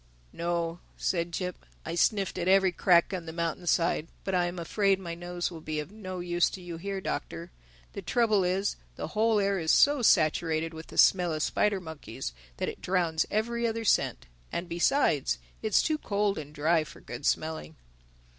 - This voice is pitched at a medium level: Yes, medium, 175 Hz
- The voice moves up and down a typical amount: Yes, average, 3.4 semitones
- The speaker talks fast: No, average, 185 wpm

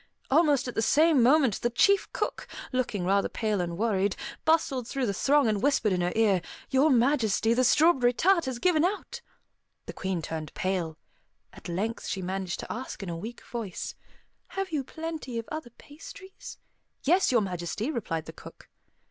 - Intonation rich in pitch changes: Yes, wide, 7.2 semitones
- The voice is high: Yes, high, 235 Hz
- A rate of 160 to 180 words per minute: Yes, average, 175 wpm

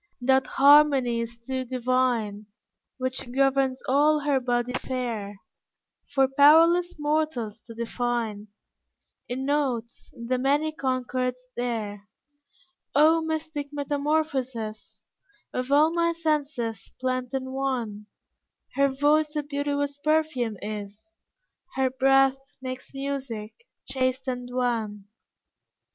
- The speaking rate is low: Yes, slow, 105 wpm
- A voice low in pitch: No, very high, 260 Hz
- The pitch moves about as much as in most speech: Yes, average, 3.1 semitones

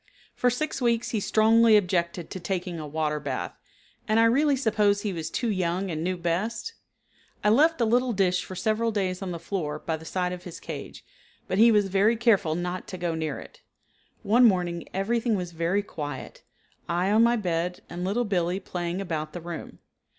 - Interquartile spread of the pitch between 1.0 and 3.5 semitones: No, average, 4.3 semitones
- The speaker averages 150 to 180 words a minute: No, average, 195 wpm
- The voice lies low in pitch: No, medium, 185 Hz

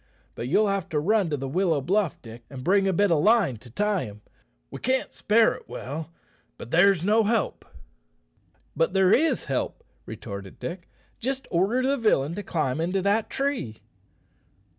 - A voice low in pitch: No, medium, 185 Hz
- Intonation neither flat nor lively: No, wide, 6.5 semitones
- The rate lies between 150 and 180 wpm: Yes, average, 175 wpm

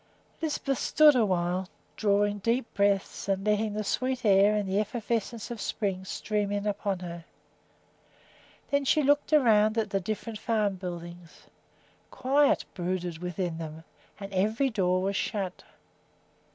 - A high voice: Yes, high, 205 Hz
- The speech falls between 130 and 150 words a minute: Yes, average, 140 wpm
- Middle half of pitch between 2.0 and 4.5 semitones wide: Yes, average, 3.4 semitones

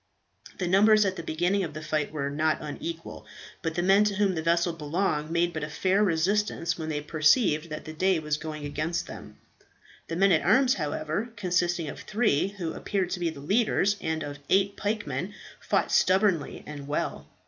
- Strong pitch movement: No, average, 4.0 semitones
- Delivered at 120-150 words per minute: No, average, 190 wpm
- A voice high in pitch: No, medium, 170 Hz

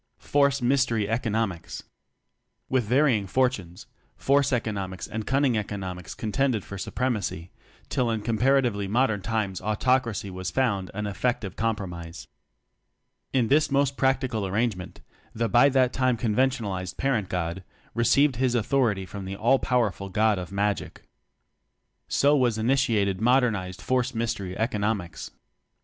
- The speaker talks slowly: Yes, slow, 130 wpm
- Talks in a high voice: No, low, 110 Hz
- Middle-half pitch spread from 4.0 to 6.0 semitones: Yes, average, 4.6 semitones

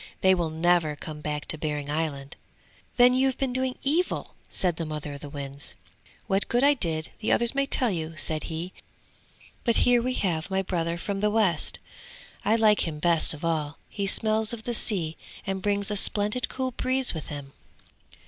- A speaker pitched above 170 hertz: Yes, medium, 185 Hz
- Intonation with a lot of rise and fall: Yes, wide, 6.5 semitones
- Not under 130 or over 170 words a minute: No, average, 190 wpm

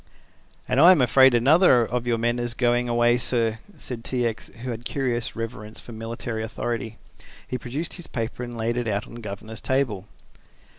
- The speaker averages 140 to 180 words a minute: No, average, 190 wpm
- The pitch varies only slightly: Yes, narrow, 1.7 semitones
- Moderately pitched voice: No, low, 120 Hz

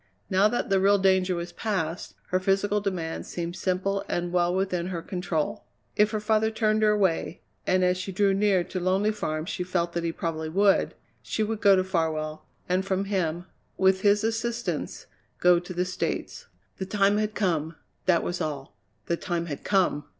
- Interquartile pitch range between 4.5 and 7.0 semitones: No, average, 2.7 semitones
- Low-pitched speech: No, medium, 185 Hz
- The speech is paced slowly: No, average, 185 wpm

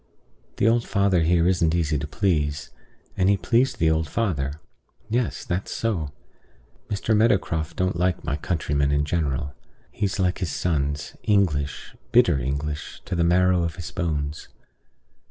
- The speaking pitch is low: Yes, very low, 85 Hz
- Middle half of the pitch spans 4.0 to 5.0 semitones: Yes, average, 4.5 semitones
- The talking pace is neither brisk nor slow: Yes, average, 150 wpm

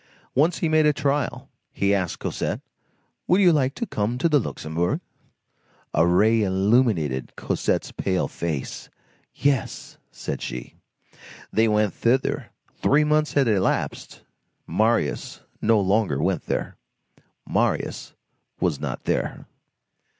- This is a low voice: Yes, low, 110 Hz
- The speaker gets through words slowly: Yes, slow, 120 wpm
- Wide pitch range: Yes, wide, 7.2 semitones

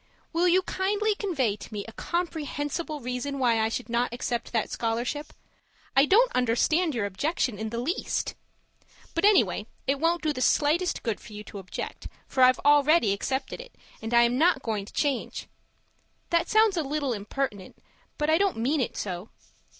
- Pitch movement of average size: No, wide, 6.4 semitones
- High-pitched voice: Yes, very high, 270 Hz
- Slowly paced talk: No, average, 180 wpm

